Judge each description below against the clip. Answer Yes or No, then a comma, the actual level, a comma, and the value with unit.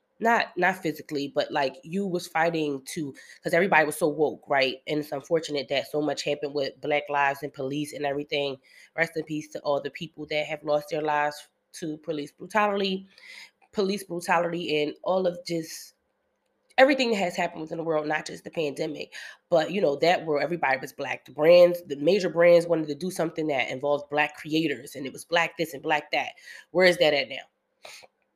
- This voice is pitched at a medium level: Yes, medium, 155 Hz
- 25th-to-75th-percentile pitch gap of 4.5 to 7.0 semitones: No, average, 3.0 semitones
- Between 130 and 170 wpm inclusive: No, average, 200 wpm